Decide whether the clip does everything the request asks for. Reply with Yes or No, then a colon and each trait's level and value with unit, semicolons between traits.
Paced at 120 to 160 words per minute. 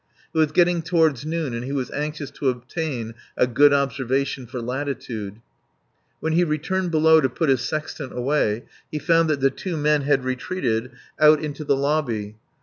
No: average, 175 wpm